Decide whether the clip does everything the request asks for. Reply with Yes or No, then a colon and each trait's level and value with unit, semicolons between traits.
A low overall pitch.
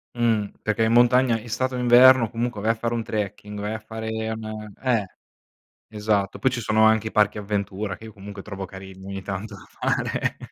Yes: low, 110 Hz